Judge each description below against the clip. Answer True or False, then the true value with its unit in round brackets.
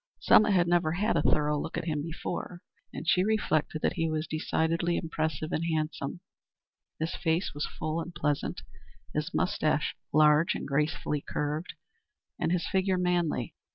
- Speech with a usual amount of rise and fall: False (2.3 semitones)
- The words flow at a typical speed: True (155 wpm)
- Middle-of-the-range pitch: True (160 Hz)